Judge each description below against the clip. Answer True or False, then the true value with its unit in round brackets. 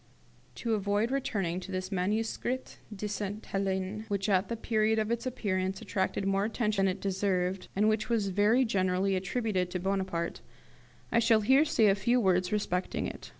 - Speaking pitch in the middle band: False (200 Hz)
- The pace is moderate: True (175 wpm)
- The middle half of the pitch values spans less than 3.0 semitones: True (2.6 semitones)